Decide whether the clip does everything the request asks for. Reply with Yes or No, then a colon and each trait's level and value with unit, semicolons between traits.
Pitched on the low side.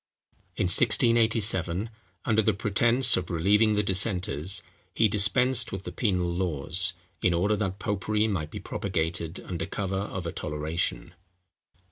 Yes: very low, 95 Hz